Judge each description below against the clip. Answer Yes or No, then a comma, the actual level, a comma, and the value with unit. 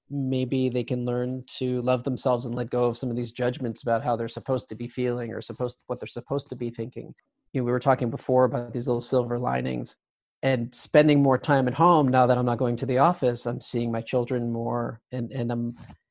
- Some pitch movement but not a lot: No, narrow, 1.4 semitones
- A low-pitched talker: Yes, low, 125 Hz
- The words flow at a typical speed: No, fast, 235 wpm